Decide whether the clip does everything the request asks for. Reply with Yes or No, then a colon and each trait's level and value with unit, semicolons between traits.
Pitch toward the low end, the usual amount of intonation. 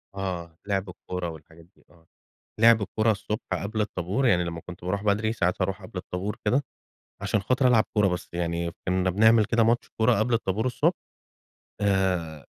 Yes: very low, 95 Hz; average, 3.7 semitones